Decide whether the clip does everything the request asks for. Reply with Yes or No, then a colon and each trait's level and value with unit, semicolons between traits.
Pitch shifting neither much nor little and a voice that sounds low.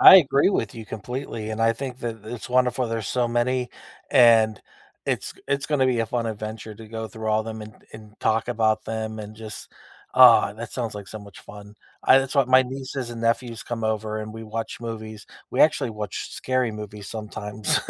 No: narrow, 2.3 semitones; low, 115 Hz